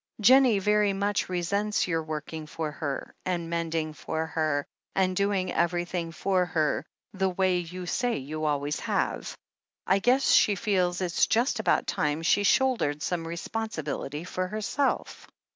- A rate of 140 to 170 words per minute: Yes, average, 150 wpm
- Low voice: No, medium, 180 Hz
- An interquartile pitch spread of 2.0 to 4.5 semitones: Yes, average, 4.1 semitones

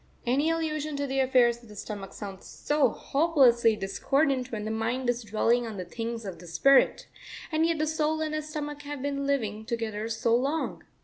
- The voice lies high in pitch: Yes, very high, 250 Hz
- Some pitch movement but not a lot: Yes, average, 4.9 semitones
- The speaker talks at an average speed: Yes, average, 195 wpm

